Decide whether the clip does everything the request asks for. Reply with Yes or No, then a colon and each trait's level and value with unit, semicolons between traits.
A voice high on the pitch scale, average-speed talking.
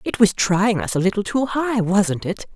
No: high, 200 Hz; fast, 235 wpm